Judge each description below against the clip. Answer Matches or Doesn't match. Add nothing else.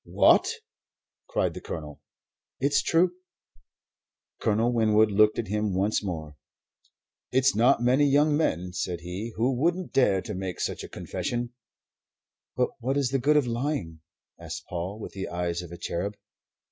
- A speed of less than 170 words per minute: Matches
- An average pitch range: Doesn't match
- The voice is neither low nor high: Doesn't match